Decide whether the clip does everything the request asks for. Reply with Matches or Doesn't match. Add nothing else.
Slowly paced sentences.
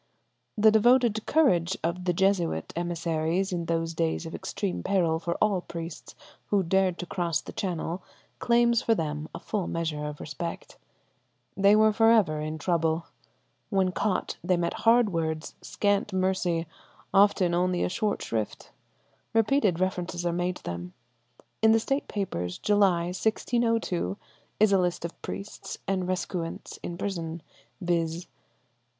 Doesn't match